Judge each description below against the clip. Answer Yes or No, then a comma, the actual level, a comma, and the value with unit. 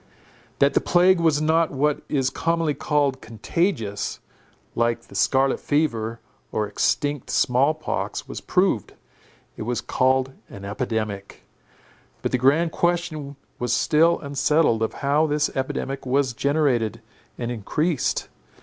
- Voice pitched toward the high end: No, medium, 140 Hz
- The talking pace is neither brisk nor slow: No, slow, 130 wpm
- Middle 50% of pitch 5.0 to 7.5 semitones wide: No, average, 4.6 semitones